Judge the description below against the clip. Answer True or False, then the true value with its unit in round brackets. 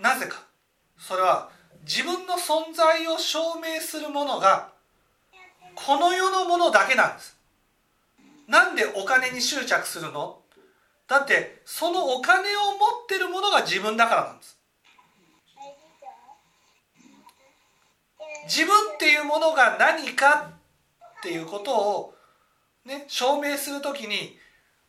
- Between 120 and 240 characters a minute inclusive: True (220 characters per minute)